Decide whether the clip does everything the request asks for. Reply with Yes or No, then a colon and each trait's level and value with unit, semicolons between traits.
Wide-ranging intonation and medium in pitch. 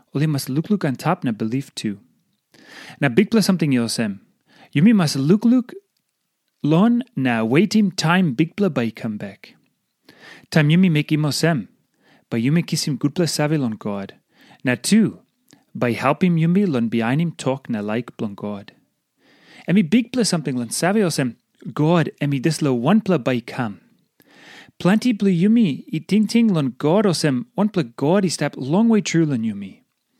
Yes: wide, 6.8 semitones; medium, 160 Hz